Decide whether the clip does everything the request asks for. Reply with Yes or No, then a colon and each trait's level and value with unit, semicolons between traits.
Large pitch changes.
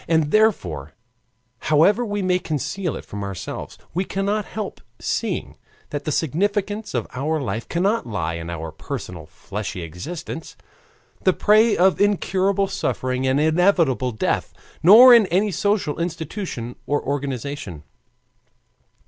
Yes: wide, 8.1 semitones